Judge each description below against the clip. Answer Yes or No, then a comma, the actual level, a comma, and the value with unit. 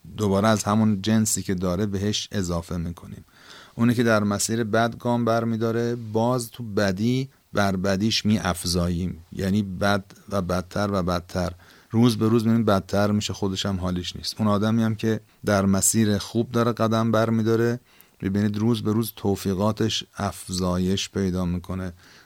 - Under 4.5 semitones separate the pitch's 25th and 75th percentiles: Yes, average, 2.9 semitones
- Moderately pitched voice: No, low, 105 Hz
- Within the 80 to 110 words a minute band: No, fast, 155 wpm